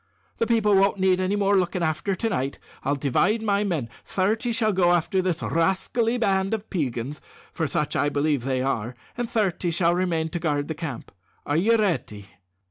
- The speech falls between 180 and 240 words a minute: Yes, average, 190 wpm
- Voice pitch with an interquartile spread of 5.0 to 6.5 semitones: Yes, average, 5.3 semitones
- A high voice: No, medium, 180 Hz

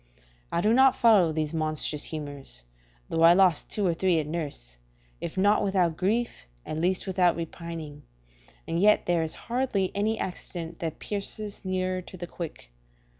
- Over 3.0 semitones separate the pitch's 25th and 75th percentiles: Yes, average, 3.7 semitones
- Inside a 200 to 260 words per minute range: No, average, 165 wpm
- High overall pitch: No, medium, 175 Hz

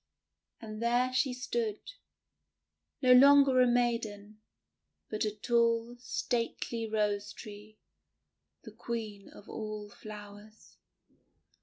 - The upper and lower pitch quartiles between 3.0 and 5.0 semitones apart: No, narrow, 2.4 semitones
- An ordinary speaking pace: No, slow, 100 wpm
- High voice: Yes, high, 225 Hz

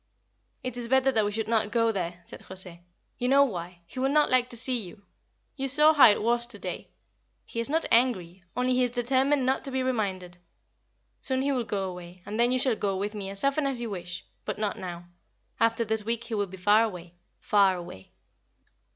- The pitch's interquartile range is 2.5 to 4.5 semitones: No, average, 5.2 semitones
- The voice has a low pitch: No, high, 225 Hz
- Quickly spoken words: Yes, fast, 220 wpm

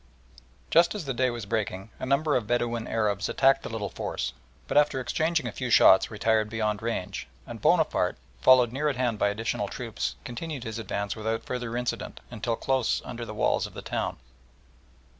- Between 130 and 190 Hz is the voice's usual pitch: No, low, 115 Hz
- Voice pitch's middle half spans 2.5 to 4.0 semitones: Yes, average, 3.2 semitones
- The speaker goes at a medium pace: Yes, average, 185 wpm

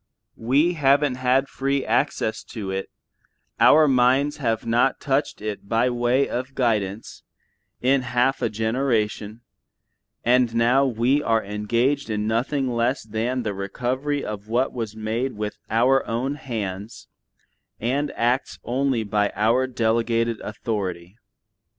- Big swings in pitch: No, average, 3.4 semitones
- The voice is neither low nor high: No, low, 120 Hz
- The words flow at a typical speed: No, slow, 130 wpm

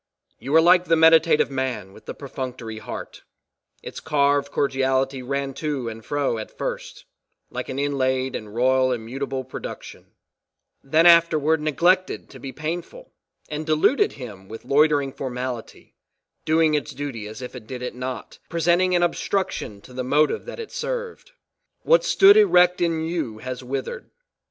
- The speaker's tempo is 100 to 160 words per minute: Yes, average, 155 wpm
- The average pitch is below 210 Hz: Yes, medium, 140 Hz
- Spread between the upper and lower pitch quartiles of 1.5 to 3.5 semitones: No, average, 4.3 semitones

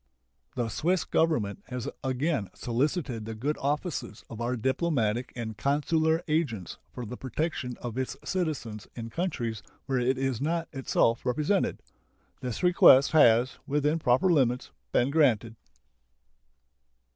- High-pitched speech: No, low, 130 Hz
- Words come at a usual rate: No, slow, 130 wpm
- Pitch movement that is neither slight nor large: Yes, average, 4.8 semitones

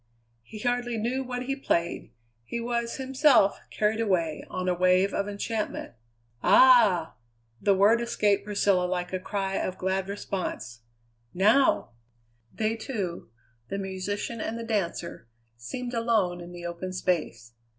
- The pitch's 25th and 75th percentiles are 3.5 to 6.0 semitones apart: Yes, average, 4.3 semitones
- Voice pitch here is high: Yes, high, 200 Hz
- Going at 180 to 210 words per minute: No, average, 140 wpm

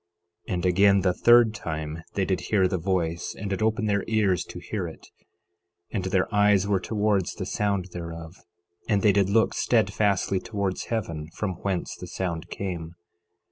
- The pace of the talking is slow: No, average, 175 wpm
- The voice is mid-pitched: No, very low, 95 Hz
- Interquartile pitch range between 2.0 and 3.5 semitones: Yes, average, 2.7 semitones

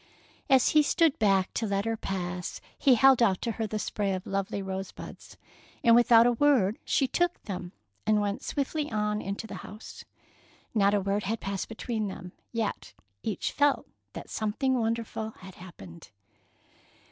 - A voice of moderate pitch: No, high, 215 Hz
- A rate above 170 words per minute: No, average, 165 wpm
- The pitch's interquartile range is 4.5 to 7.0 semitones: No, average, 3.4 semitones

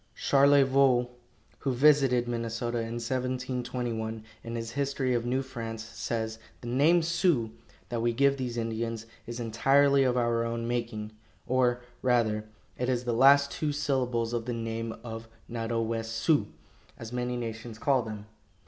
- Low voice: Yes, low, 120 Hz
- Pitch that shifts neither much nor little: No, narrow, 2.3 semitones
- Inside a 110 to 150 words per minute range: Yes, average, 145 wpm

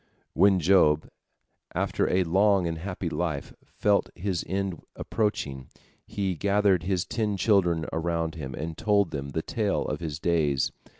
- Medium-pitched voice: No, very low, 90 Hz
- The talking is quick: No, average, 155 wpm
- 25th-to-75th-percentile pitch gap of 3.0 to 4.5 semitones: Yes, average, 3.6 semitones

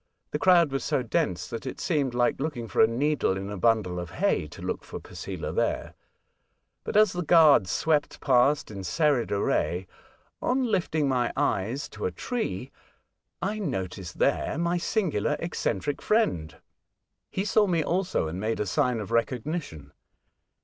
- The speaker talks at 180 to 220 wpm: No, average, 165 wpm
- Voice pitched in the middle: No, low, 130 Hz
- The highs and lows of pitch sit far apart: Yes, wide, 8.5 semitones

